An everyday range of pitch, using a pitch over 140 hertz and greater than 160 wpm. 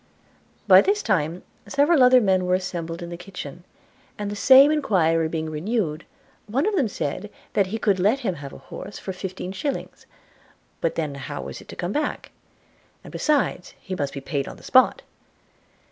No: wide, 6.9 semitones; high, 190 Hz; average, 185 wpm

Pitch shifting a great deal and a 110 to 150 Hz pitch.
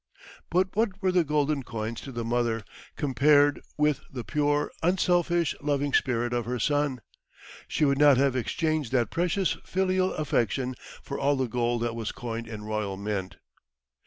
No: average, 4.5 semitones; medium, 140 Hz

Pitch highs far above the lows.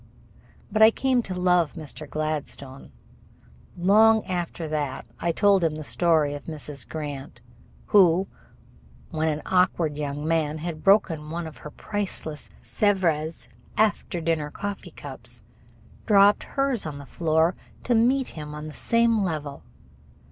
No: average, 4.7 semitones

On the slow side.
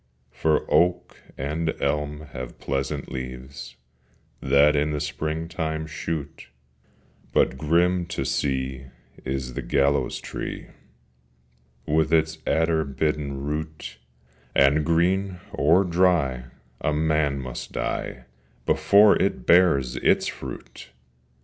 Yes: slow, 105 wpm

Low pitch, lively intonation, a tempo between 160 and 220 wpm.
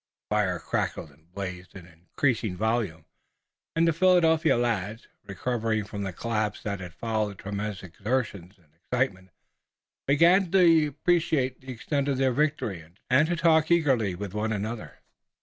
No: low, 110 Hz; wide, 6.7 semitones; average, 150 wpm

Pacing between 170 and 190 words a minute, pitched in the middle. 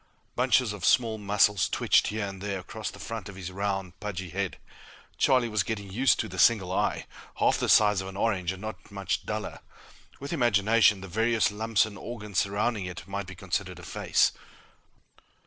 No: average, 185 wpm; low, 105 Hz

